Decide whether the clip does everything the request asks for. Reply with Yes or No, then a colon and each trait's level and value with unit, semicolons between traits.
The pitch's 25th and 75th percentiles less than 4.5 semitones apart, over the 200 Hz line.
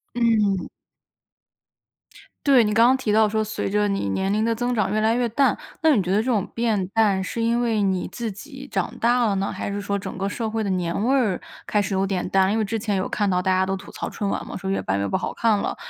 Yes: average, 3.0 semitones; high, 210 Hz